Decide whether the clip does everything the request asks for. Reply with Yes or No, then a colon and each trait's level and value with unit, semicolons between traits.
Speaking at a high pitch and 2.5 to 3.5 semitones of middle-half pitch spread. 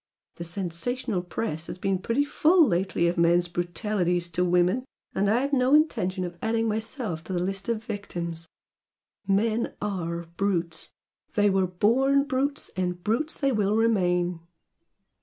No: high, 195 Hz; average, 4.6 semitones